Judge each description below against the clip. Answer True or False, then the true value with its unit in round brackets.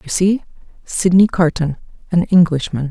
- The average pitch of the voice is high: False (170 Hz)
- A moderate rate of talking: False (105 wpm)